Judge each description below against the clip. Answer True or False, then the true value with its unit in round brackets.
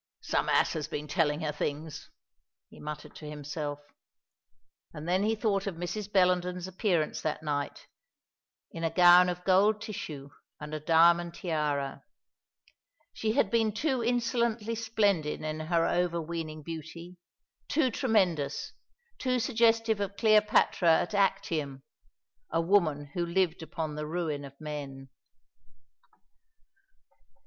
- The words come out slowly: True (125 wpm)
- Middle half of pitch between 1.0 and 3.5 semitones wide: False (5.0 semitones)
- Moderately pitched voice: True (170 Hz)